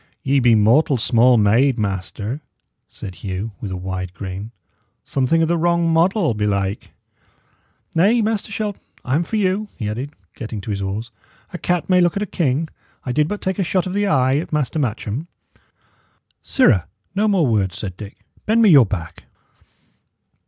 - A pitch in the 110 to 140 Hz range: Yes, low, 135 Hz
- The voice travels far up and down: Yes, wide, 8.9 semitones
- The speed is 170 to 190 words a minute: Yes, average, 175 wpm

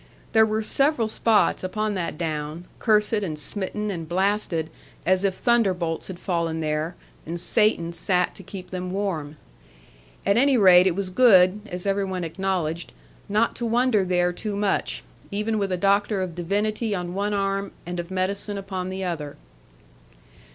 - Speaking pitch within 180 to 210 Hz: Yes, high, 190 Hz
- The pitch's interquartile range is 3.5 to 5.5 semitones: No, average, 2.9 semitones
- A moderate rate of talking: Yes, average, 165 wpm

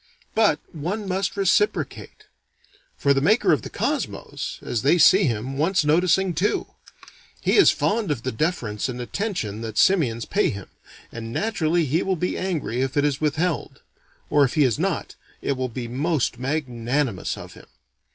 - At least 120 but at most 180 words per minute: Yes, average, 170 wpm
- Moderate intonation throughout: No, wide, 6.6 semitones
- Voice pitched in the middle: Yes, medium, 150 Hz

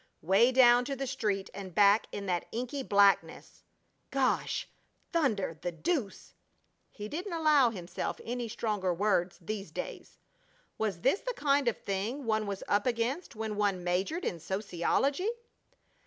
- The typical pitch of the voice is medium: No, high, 215 Hz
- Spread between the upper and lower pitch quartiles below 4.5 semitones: No, average, 5.3 semitones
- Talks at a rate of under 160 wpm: Yes, average, 145 wpm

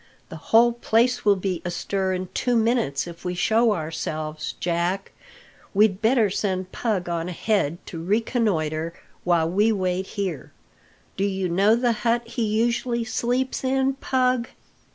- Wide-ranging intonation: No, average, 4.8 semitones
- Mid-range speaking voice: No, high, 200 Hz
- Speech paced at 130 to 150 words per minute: Yes, average, 145 wpm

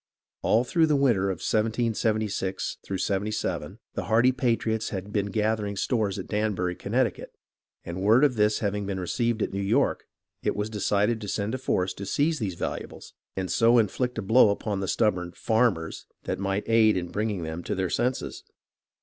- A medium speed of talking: Yes, average, 185 wpm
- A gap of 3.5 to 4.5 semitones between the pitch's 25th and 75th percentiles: No, average, 2.9 semitones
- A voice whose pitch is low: Yes, low, 105 Hz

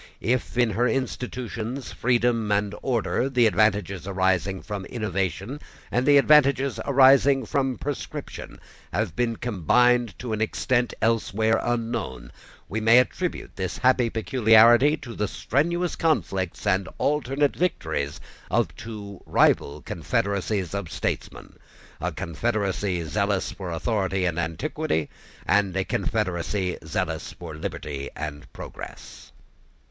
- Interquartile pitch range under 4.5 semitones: No, average, 4.9 semitones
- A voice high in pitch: No, low, 110 Hz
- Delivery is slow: Yes, slow, 120 wpm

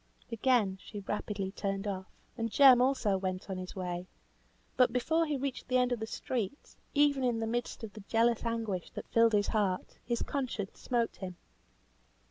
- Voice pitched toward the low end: No, high, 225 Hz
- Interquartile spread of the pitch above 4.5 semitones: No, average, 4.2 semitones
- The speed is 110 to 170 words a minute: No, average, 180 wpm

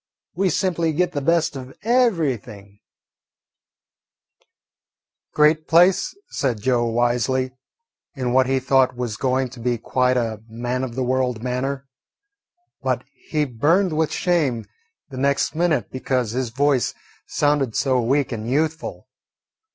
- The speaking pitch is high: No, low, 130 Hz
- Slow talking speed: Yes, slow, 130 wpm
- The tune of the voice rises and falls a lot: No, average, 3.8 semitones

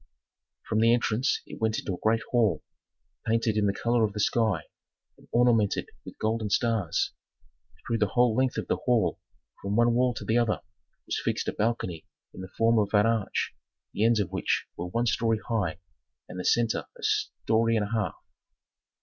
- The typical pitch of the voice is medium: No, low, 110 Hz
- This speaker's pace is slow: No, average, 190 wpm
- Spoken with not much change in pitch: Yes, narrow, 2.2 semitones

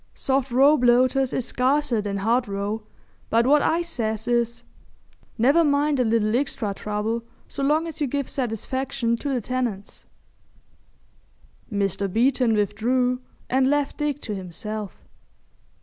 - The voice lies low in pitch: No, high, 245 Hz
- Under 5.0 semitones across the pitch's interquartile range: Yes, average, 4.1 semitones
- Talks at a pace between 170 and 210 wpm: No, slow, 135 wpm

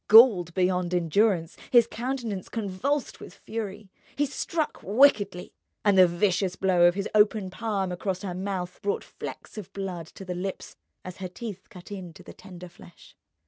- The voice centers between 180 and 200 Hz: Yes, high, 190 Hz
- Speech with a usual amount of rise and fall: Yes, average, 3.0 semitones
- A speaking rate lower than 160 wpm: No, average, 165 wpm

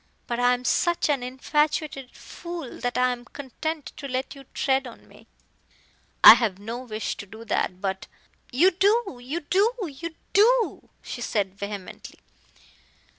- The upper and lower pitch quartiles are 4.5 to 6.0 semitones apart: Yes, average, 5.2 semitones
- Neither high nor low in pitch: No, very high, 260 Hz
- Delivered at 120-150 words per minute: No, average, 160 wpm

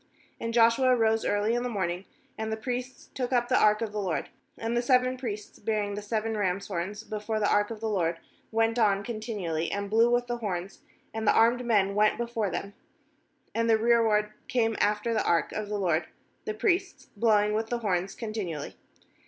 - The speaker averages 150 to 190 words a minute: No, fast, 205 wpm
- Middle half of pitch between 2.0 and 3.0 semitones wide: Yes, narrow, 2.4 semitones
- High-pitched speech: Yes, high, 220 Hz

